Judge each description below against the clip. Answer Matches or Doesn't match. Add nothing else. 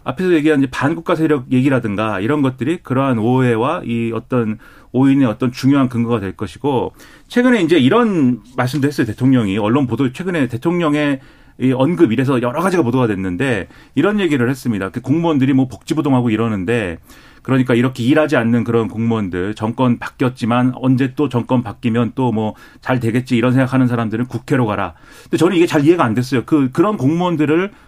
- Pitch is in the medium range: Doesn't match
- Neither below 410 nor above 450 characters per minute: Matches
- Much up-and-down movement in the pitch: Doesn't match